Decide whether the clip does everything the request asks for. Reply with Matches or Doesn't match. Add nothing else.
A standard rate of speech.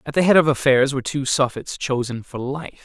Doesn't match